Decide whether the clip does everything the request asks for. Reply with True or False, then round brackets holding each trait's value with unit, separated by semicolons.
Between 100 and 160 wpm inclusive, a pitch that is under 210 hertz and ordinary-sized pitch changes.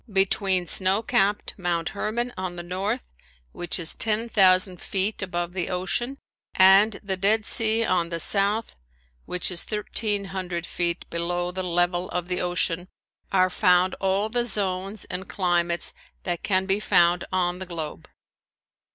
False (150 wpm; 185 Hz; 2.2 semitones)